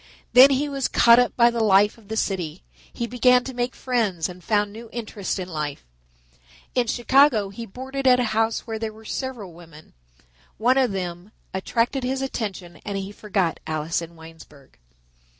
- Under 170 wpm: No, average, 180 wpm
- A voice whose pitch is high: Yes, high, 220 Hz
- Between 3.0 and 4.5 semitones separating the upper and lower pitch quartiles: No, average, 5.1 semitones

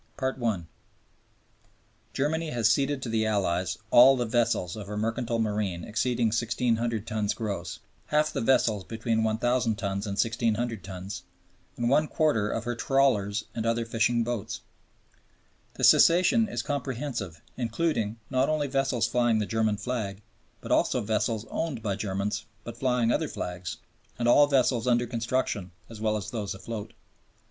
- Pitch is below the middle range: Yes, low, 115 Hz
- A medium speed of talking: Yes, average, 155 wpm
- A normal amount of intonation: Yes, average, 3.1 semitones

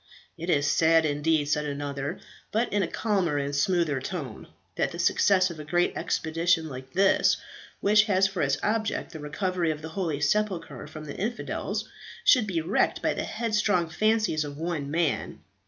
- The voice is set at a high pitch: No, medium, 165 Hz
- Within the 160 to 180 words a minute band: Yes, average, 175 wpm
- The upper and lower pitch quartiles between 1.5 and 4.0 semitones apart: No, average, 4.7 semitones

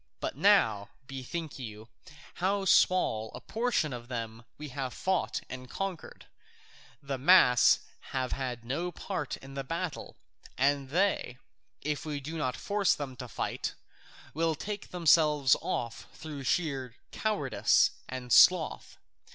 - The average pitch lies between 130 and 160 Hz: Yes, medium, 140 Hz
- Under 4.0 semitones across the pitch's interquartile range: No, average, 5.2 semitones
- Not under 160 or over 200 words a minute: No, slow, 135 wpm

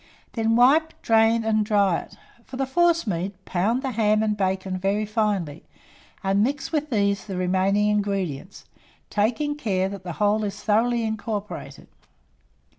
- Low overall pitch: No, high, 210 Hz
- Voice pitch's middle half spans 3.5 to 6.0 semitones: No, average, 2.9 semitones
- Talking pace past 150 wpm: No, average, 145 wpm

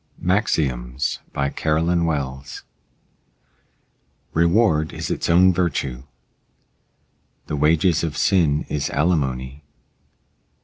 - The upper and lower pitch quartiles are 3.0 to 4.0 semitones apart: Yes, average, 3.6 semitones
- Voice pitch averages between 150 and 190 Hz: No, very low, 75 Hz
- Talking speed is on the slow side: Yes, slow, 85 wpm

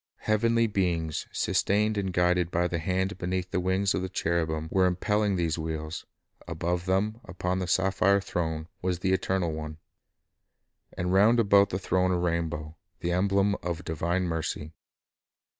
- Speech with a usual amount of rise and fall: No, narrow, 2.3 semitones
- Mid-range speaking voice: No, very low, 90 Hz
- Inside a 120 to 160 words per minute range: Yes, average, 155 wpm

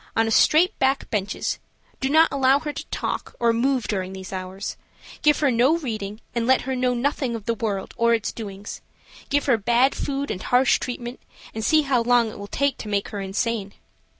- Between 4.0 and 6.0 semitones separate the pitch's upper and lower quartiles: Yes, average, 4.4 semitones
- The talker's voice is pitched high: Yes, high, 235 Hz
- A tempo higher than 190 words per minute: Yes, fast, 205 wpm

